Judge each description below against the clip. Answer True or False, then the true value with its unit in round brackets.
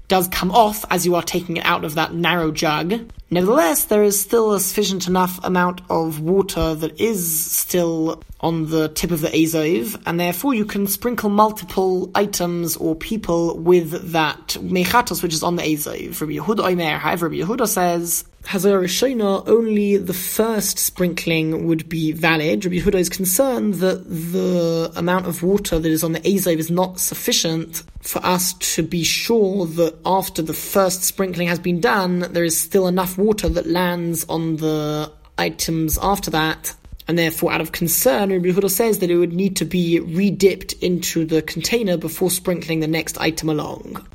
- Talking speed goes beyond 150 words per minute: True (170 wpm)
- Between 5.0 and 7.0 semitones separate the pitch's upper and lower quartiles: False (2.8 semitones)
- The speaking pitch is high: False (175 Hz)